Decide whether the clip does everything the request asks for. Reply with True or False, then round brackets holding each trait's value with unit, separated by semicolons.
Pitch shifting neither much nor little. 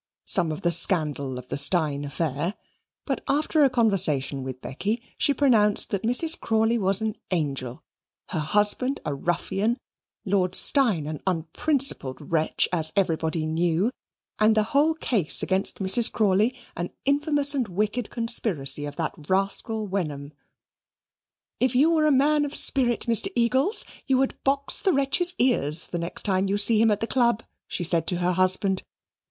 False (7.3 semitones)